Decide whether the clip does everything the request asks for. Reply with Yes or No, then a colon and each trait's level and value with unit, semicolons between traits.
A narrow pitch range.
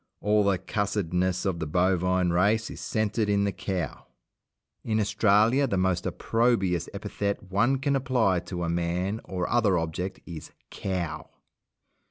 No: average, 3.1 semitones